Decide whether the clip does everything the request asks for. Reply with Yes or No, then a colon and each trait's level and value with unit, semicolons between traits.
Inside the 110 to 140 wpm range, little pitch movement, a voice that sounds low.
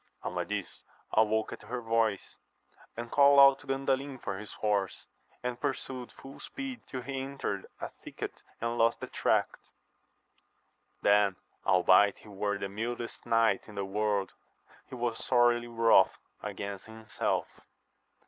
No: slow, 135 wpm; average, 3.8 semitones; low, 115 Hz